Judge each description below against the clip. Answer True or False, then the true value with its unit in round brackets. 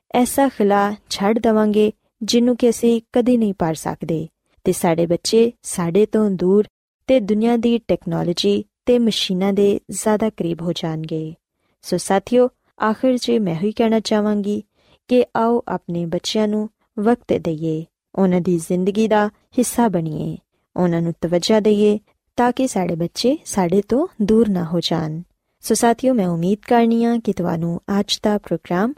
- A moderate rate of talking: True (150 wpm)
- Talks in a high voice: True (210 Hz)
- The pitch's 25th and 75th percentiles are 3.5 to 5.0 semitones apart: True (4.6 semitones)